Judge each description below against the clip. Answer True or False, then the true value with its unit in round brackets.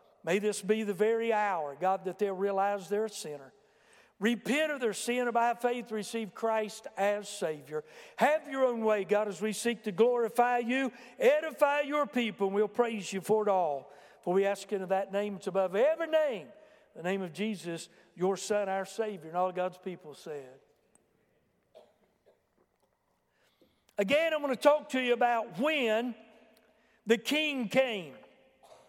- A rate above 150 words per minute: True (165 wpm)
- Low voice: False (215 Hz)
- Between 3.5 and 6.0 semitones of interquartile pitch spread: True (3.9 semitones)